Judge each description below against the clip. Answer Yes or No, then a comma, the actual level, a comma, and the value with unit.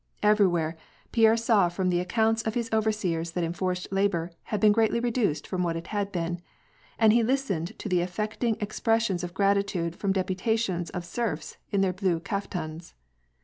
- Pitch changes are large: No, average, 4.0 semitones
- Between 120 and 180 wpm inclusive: Yes, average, 170 wpm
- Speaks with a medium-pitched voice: No, high, 195 Hz